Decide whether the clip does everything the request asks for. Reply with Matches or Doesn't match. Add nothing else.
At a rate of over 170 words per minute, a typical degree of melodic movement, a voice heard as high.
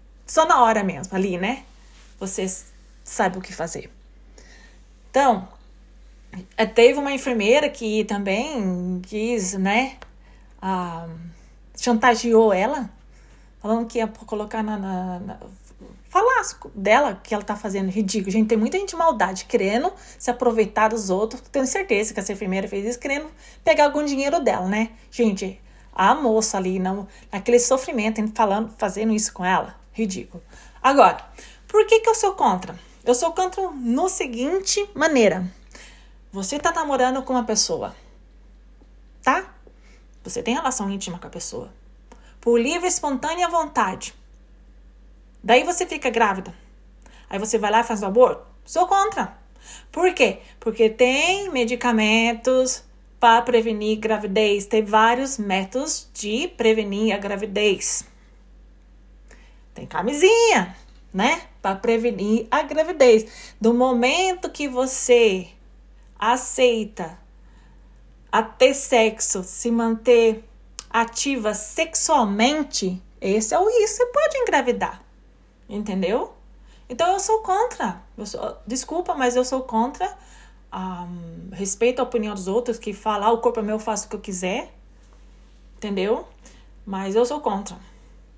Doesn't match